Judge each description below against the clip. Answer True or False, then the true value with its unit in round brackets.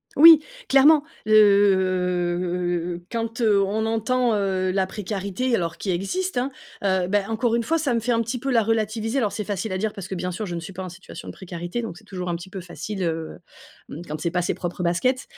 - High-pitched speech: True (200 Hz)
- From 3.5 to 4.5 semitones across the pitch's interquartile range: True (4.0 semitones)